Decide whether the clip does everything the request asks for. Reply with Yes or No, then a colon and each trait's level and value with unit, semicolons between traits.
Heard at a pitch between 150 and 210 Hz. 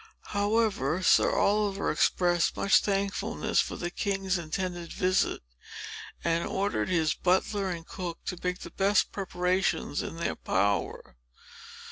Yes: medium, 185 Hz